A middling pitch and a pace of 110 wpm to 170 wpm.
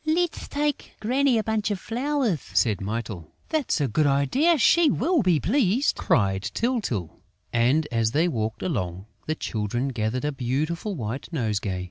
Yes: medium, 150 Hz; average, 155 wpm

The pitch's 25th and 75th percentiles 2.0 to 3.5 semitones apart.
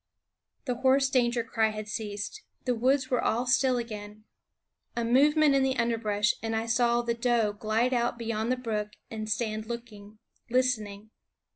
Yes: narrow, 2.6 semitones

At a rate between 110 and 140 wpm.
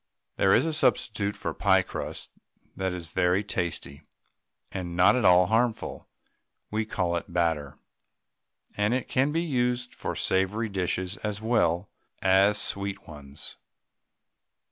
Yes: slow, 135 wpm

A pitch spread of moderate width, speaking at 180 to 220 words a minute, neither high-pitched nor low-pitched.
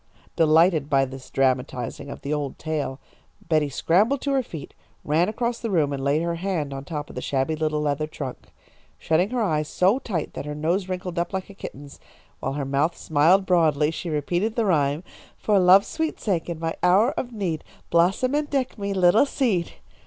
Yes: average, 4.9 semitones; average, 195 wpm; medium, 165 Hz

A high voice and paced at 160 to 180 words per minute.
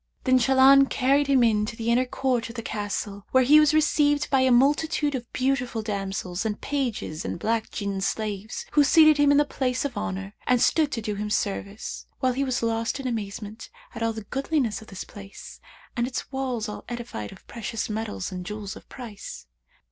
No: high, 235 Hz; average, 195 wpm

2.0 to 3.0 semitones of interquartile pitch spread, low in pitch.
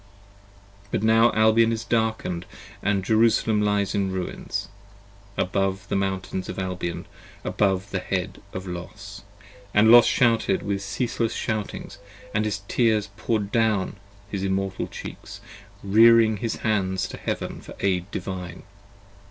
Yes: average, 2.7 semitones; low, 100 Hz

